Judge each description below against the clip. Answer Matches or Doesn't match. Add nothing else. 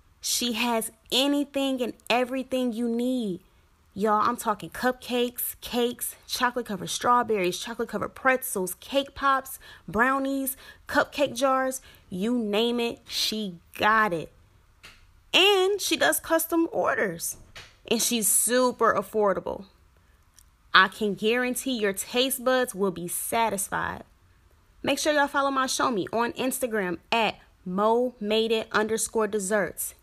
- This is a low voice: Doesn't match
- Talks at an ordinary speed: Doesn't match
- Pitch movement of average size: Matches